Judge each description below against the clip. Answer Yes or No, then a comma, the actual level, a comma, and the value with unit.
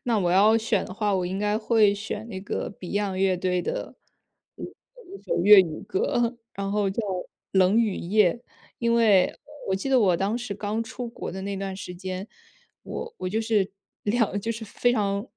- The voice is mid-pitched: No, high, 205 Hz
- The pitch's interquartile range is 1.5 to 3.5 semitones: Yes, average, 3.1 semitones